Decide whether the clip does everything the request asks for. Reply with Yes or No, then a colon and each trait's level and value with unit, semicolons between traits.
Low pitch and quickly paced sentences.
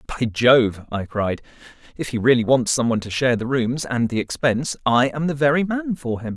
Yes: low, 125 Hz; fast, 215 wpm